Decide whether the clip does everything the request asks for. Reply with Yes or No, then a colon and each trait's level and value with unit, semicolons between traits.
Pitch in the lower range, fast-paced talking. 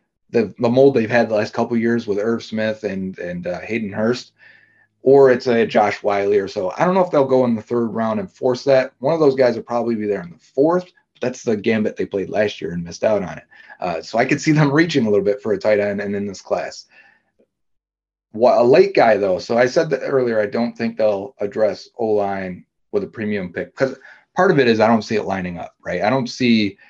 Yes: low, 115 Hz; fast, 260 wpm